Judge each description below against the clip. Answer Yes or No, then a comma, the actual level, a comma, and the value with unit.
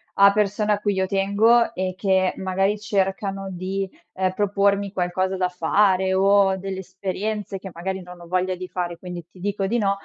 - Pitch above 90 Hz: Yes, high, 190 Hz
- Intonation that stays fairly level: Yes, narrow, 1.4 semitones